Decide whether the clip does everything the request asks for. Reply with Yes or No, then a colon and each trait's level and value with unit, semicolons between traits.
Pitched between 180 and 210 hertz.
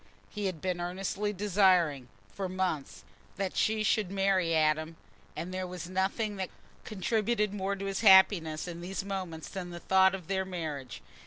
Yes: high, 190 Hz